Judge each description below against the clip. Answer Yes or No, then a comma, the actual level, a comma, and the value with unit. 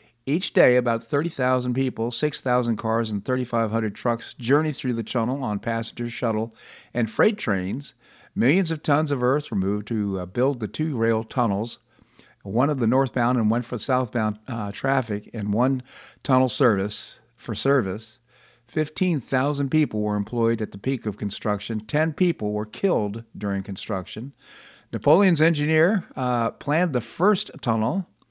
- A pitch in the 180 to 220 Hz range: No, low, 120 Hz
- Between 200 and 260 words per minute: No, average, 150 wpm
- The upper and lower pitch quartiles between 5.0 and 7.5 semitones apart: No, average, 4.1 semitones